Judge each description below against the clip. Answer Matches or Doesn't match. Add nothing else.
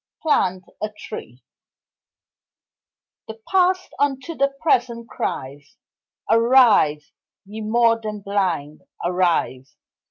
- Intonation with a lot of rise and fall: Matches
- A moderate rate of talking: Doesn't match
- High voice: Matches